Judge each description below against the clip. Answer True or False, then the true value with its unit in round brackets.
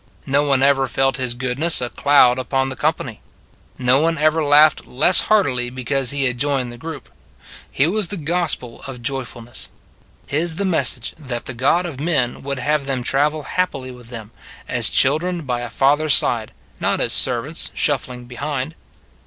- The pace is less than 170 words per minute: False (175 wpm)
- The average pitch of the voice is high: False (135 Hz)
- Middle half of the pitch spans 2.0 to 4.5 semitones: True (3.5 semitones)